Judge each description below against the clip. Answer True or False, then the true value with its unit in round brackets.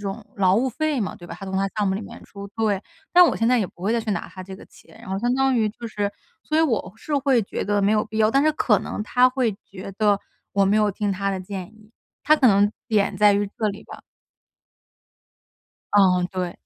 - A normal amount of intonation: True (3.0 semitones)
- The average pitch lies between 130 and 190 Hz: False (210 Hz)